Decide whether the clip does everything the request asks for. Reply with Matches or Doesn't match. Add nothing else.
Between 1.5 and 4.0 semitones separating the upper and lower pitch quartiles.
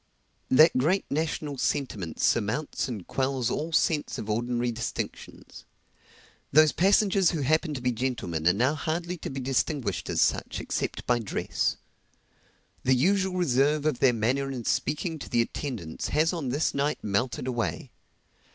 Doesn't match